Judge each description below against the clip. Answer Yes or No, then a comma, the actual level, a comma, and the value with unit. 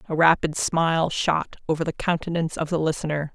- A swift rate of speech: No, average, 180 wpm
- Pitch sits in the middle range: Yes, medium, 160 Hz